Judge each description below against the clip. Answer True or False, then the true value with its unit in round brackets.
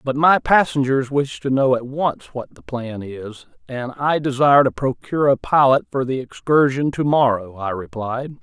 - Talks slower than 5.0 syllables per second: True (4.7 syllables/s)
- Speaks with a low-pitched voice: True (130 Hz)